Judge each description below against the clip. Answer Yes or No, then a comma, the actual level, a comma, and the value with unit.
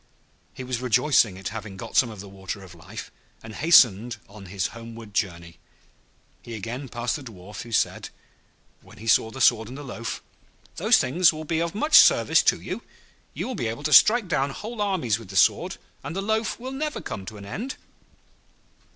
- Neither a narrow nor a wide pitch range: No, wide, 7.5 semitones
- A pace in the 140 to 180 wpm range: No, average, 200 wpm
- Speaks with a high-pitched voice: No, low, 115 Hz